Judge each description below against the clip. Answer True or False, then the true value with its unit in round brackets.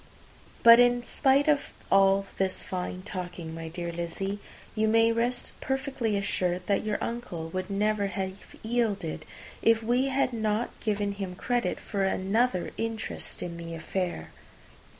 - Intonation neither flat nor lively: True (4.1 semitones)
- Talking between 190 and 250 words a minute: False (145 wpm)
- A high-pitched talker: True (205 Hz)